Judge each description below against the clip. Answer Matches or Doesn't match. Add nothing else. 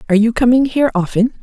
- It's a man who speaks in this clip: Doesn't match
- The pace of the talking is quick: Matches